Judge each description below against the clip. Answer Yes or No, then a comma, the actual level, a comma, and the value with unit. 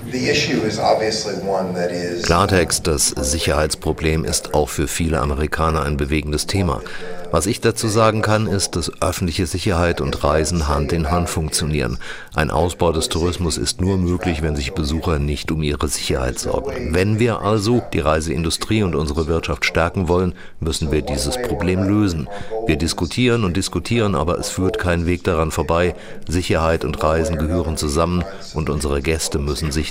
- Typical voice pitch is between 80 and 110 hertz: Yes, very low, 85 Hz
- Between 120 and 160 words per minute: Yes, average, 155 wpm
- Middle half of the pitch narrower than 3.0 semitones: No, average, 3.3 semitones